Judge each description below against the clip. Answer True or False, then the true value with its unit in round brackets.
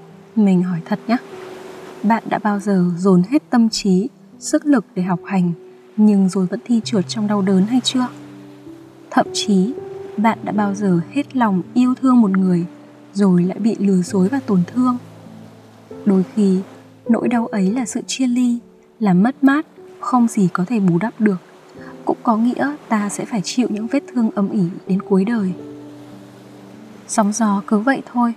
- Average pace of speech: True (180 wpm)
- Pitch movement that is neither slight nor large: True (4.6 semitones)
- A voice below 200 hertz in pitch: False (205 Hz)